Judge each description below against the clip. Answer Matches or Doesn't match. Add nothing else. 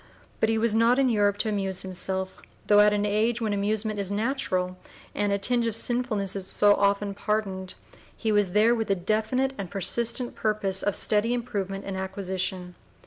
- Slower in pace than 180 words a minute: Doesn't match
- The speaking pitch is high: Matches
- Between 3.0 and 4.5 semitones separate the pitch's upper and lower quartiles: Doesn't match